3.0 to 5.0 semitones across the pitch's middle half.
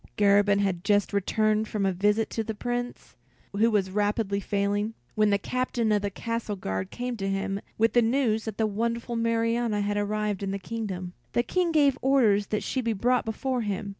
No: narrow, 2.5 semitones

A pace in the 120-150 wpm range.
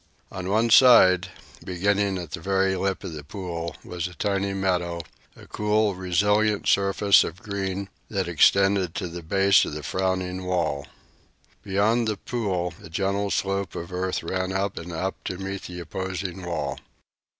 No: average, 160 wpm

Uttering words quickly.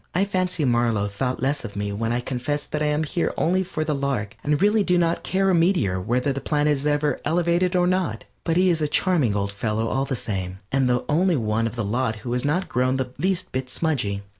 Yes: fast, 240 wpm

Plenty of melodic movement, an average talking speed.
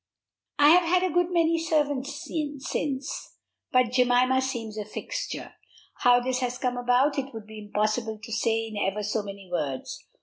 No: average, 4.7 semitones; average, 170 wpm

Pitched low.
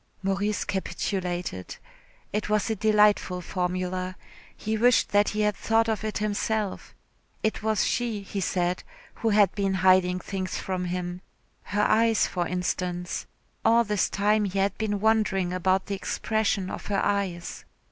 No: high, 200 Hz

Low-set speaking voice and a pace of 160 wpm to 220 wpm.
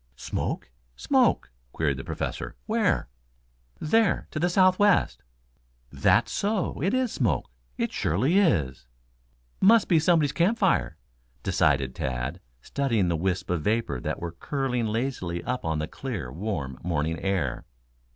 No: low, 105 Hz; slow, 135 wpm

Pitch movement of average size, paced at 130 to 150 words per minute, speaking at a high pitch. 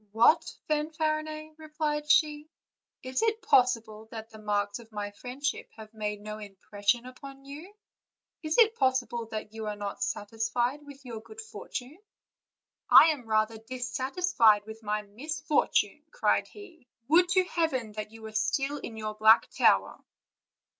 No: wide, 5.8 semitones; average, 145 wpm; high, 245 Hz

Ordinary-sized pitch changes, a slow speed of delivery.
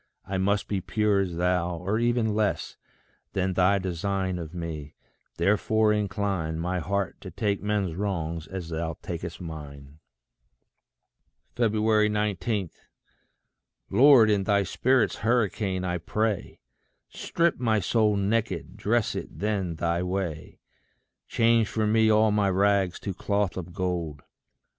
Yes: average, 3.4 semitones; slow, 130 wpm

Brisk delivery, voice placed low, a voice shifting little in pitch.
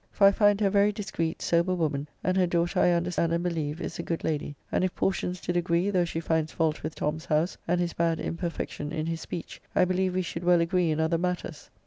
No: fast, 245 wpm; medium, 170 Hz; narrow, 2.0 semitones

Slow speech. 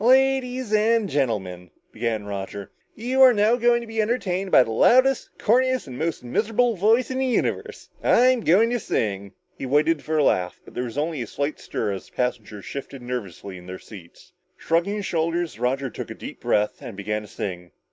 No: average, 200 wpm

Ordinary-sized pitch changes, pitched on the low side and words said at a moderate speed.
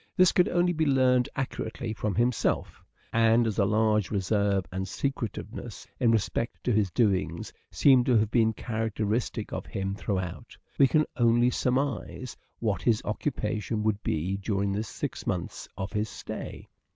Yes: average, 3.5 semitones; low, 110 Hz; average, 155 wpm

